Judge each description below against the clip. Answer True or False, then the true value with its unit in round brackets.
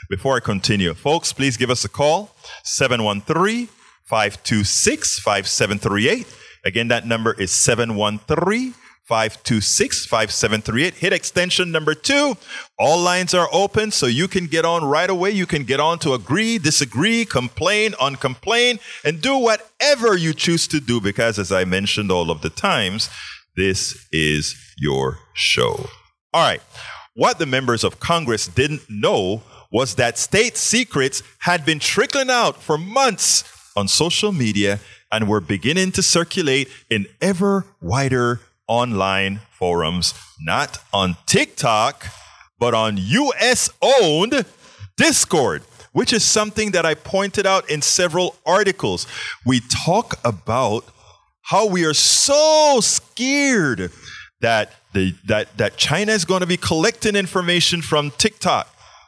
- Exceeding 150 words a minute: False (135 wpm)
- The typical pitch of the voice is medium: True (145 Hz)